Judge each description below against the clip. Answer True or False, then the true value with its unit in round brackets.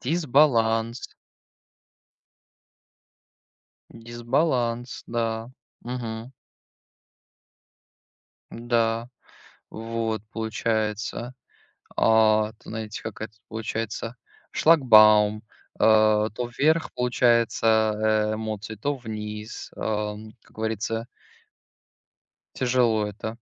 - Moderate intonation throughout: False (1.7 semitones)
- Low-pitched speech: True (110 Hz)